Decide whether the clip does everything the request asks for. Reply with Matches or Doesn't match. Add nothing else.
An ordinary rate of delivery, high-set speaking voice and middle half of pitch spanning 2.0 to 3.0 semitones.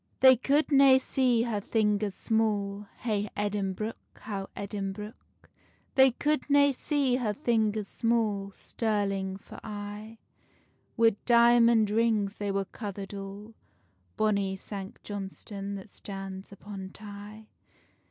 Doesn't match